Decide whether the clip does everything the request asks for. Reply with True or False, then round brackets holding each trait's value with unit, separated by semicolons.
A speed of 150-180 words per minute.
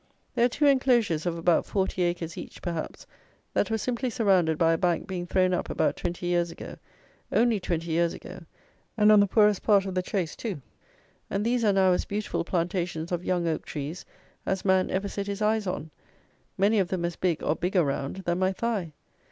False (205 wpm)